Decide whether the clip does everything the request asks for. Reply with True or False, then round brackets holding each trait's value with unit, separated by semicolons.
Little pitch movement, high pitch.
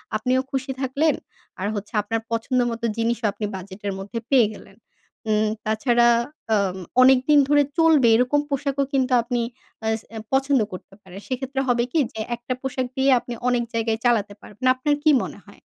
False (3.3 semitones; 245 Hz)